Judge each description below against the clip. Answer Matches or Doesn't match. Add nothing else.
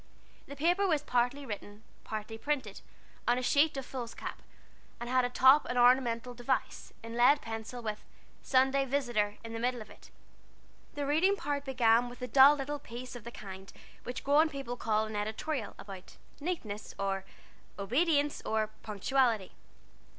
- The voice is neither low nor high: Doesn't match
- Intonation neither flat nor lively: Matches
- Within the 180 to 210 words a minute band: Doesn't match